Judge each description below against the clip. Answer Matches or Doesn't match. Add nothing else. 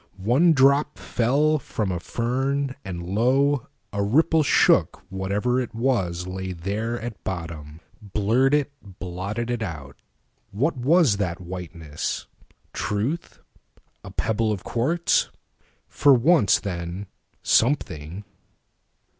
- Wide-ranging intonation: Matches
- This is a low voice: Matches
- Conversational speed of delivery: Doesn't match